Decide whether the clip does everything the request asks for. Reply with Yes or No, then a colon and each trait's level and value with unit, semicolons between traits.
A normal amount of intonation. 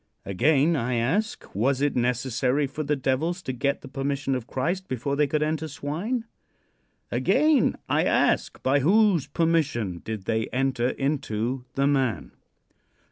Yes: average, 3.7 semitones